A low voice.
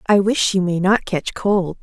No: high, 190 Hz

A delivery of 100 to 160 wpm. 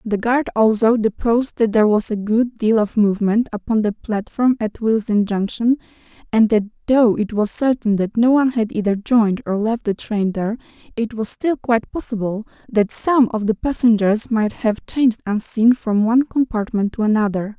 No: average, 185 wpm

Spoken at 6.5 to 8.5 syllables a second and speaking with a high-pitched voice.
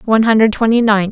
Yes: 7.1 syllables/s; high, 220 Hz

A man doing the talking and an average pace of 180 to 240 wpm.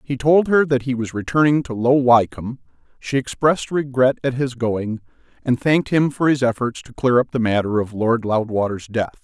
Yes: male; average, 200 wpm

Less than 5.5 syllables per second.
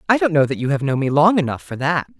No: 6.8 syllables/s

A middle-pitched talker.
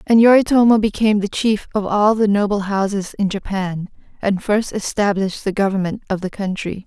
No: high, 205 Hz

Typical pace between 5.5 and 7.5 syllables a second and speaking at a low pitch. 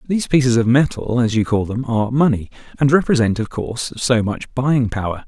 Yes: 5.7 syllables/s; low, 120 Hz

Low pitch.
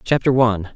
Yes: low, 115 Hz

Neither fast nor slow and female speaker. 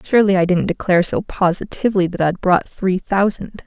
Yes: average, 180 wpm; female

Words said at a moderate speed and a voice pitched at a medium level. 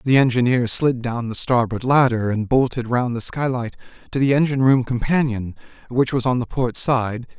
No: average, 185 wpm; low, 125 Hz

